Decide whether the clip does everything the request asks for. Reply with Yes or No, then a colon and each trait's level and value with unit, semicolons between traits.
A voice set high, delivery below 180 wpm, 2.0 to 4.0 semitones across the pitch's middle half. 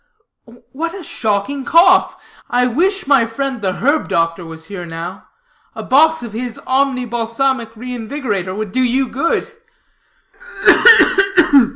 No: high, 245 Hz; average, 145 wpm; average, 4.6 semitones